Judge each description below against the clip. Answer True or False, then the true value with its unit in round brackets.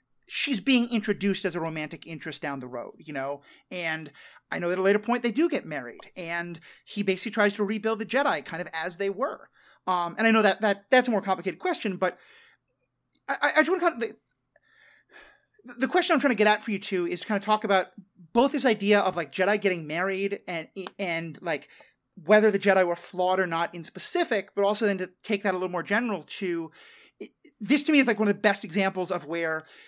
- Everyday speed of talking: False (235 wpm)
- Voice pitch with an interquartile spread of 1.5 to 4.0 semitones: False (4.6 semitones)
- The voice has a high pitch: True (200 Hz)